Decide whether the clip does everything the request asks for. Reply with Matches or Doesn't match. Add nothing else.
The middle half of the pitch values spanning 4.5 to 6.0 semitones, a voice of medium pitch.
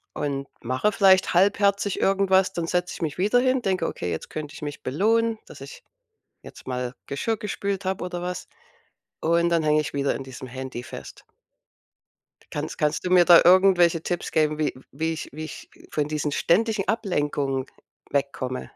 Matches